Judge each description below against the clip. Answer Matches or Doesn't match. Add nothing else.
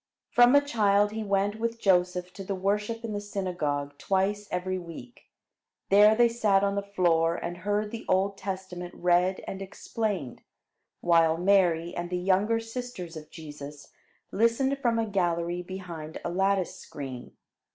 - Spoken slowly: Doesn't match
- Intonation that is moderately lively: Matches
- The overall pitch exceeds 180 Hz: Matches